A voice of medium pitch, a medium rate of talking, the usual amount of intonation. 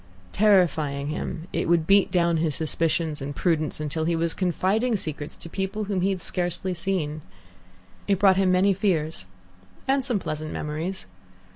Yes: medium, 170 Hz; average, 160 wpm; average, 3.7 semitones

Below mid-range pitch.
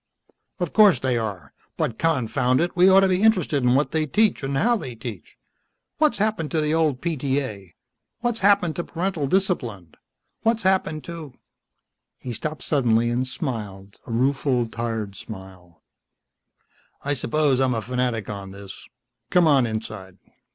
Yes: low, 130 Hz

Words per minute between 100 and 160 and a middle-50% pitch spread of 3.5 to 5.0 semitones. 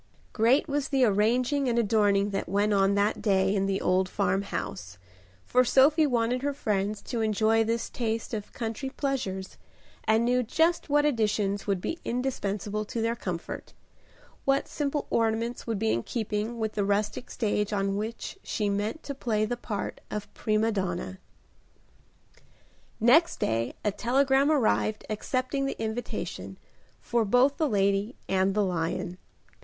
Yes: average, 150 wpm; average, 3.8 semitones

